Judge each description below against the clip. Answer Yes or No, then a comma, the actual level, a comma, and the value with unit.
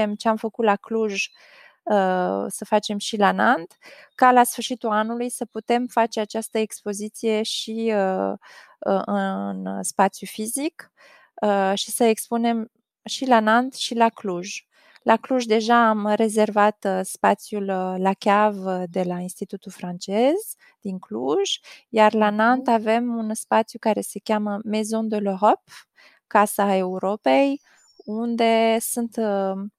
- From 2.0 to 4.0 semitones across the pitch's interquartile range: Yes, narrow, 2.5 semitones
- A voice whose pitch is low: No, high, 215 Hz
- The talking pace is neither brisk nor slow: Yes, average, 135 wpm